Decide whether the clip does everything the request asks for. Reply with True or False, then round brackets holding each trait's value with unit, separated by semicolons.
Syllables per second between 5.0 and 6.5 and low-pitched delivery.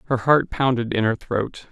False (4.7 syllables/s; 120 Hz)